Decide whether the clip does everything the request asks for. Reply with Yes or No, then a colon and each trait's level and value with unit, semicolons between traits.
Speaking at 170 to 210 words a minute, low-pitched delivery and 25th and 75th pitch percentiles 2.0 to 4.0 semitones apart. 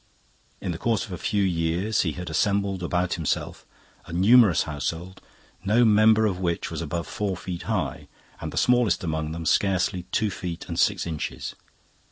Yes: average, 175 wpm; very low, 90 Hz; average, 3.5 semitones